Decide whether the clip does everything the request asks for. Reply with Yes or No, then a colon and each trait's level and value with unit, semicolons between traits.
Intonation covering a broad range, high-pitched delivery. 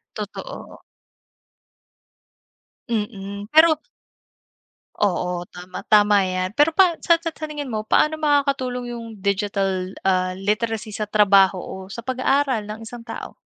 Yes: wide, 5.7 semitones; high, 215 Hz